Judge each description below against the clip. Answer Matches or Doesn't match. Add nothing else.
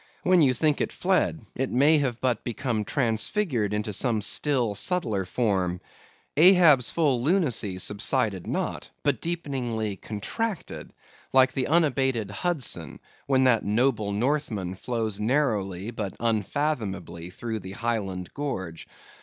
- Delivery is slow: Matches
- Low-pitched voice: Matches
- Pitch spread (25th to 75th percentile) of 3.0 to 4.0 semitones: Doesn't match